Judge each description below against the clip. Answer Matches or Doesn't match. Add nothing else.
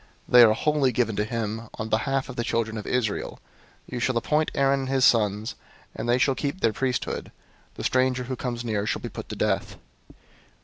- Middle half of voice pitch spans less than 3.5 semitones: Matches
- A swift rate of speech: Matches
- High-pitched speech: Doesn't match